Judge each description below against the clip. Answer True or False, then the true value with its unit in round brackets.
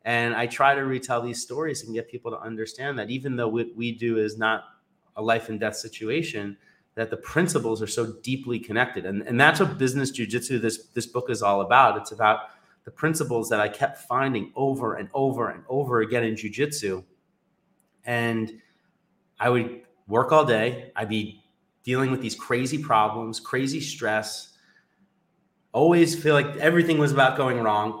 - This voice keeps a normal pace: True (180 wpm)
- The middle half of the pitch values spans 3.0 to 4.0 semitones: True (3.6 semitones)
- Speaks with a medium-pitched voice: False (120 Hz)